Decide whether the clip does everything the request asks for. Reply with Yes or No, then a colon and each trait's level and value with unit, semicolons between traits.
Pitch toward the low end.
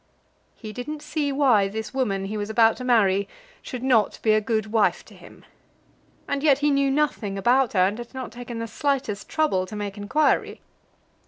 No: high, 230 Hz